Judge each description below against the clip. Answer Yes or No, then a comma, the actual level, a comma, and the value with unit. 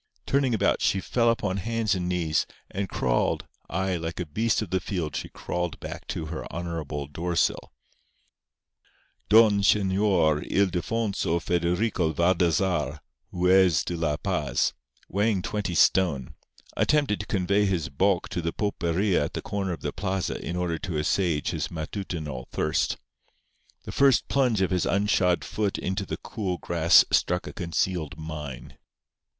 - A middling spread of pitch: Yes, average, 3.4 semitones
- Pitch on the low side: Yes, very low, 90 Hz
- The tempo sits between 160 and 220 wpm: No, average, 145 wpm